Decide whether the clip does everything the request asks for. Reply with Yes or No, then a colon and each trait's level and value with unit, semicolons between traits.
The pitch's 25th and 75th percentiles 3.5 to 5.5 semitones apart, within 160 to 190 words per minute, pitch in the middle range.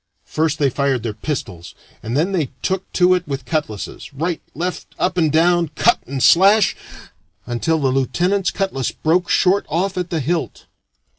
Yes: average, 5.0 semitones; average, 165 wpm; medium, 160 Hz